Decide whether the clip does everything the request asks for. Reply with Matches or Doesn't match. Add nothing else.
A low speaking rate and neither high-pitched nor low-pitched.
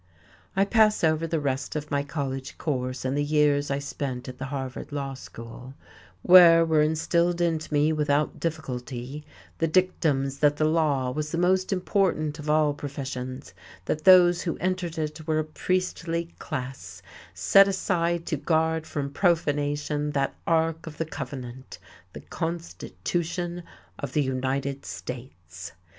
Doesn't match